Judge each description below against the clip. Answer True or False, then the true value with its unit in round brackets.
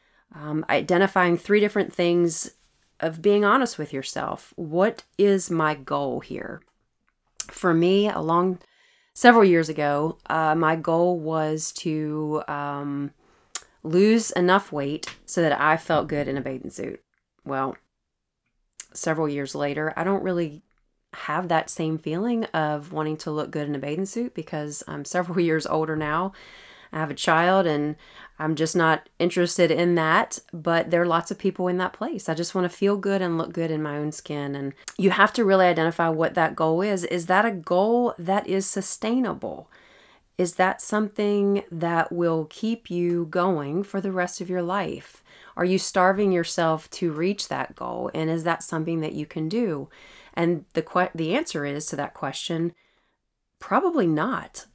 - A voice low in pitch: False (170 Hz)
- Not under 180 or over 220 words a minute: False (170 wpm)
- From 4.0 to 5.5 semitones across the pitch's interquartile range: False (3.3 semitones)